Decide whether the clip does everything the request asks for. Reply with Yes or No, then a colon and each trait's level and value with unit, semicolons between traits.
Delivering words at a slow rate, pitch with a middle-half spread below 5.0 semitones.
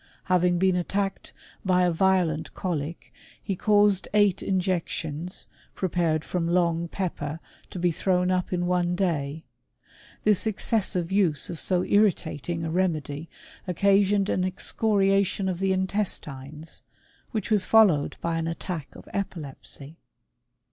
Yes: slow, 125 wpm; average, 2.9 semitones